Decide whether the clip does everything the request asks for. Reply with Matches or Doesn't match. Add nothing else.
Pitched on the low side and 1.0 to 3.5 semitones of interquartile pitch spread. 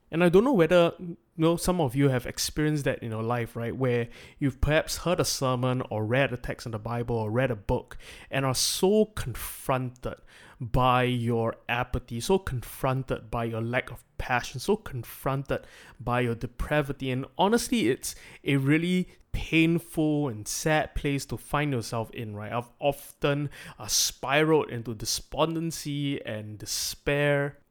Doesn't match